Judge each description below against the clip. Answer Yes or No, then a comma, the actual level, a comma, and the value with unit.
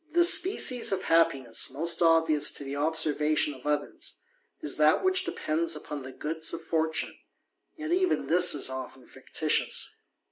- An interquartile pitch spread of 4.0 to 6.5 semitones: No, average, 3.1 semitones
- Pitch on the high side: No, medium, 160 Hz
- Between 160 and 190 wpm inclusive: No, average, 150 wpm